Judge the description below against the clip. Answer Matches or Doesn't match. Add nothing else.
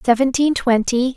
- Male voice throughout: Doesn't match